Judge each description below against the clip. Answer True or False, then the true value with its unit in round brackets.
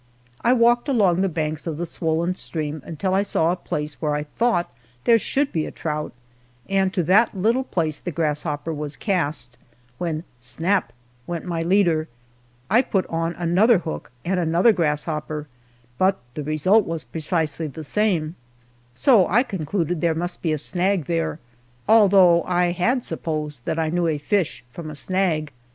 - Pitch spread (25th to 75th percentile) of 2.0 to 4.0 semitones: True (3.7 semitones)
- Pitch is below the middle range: False (170 Hz)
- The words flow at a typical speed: True (170 wpm)